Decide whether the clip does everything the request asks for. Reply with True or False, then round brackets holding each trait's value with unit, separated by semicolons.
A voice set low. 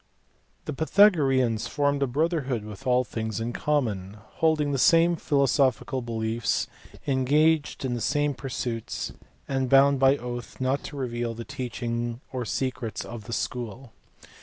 True (130 Hz)